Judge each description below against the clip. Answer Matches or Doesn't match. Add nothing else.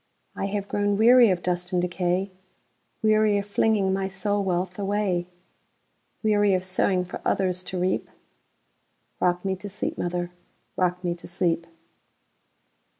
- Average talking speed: Doesn't match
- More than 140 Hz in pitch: Matches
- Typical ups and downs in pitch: Doesn't match